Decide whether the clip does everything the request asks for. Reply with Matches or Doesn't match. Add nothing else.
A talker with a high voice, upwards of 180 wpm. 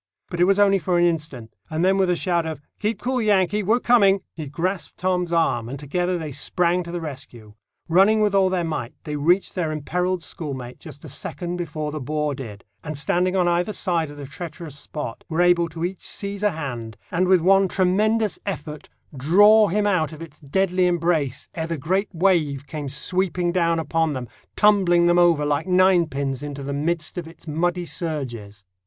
Doesn't match